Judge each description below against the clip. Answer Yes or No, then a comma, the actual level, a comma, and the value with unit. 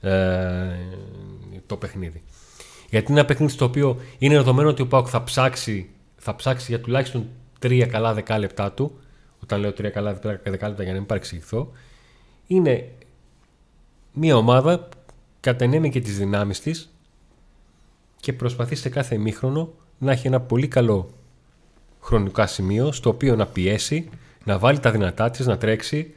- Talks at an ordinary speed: Yes, average, 145 wpm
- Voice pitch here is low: Yes, low, 120 Hz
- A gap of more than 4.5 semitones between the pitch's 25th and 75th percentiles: Yes, average, 4.9 semitones